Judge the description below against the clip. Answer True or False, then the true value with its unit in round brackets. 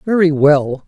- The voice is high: False (155 Hz)